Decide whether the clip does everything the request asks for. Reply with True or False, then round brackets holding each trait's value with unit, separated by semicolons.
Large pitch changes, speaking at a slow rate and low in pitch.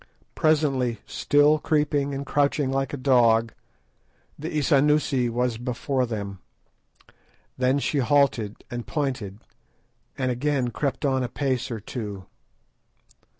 False (3.1 semitones; 115 wpm; 130 Hz)